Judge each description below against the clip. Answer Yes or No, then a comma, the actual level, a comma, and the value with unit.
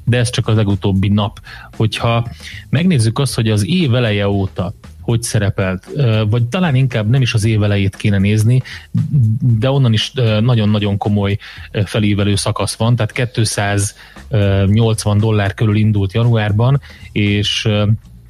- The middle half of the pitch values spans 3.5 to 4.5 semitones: No, average, 2.7 semitones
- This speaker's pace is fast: No, average, 135 wpm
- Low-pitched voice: Yes, low, 110 Hz